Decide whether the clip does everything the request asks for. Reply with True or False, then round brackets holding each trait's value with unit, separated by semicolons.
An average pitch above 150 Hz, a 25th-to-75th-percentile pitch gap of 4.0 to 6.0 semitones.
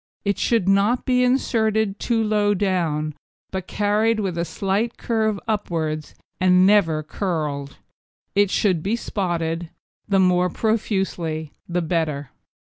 True (190 Hz; 4.3 semitones)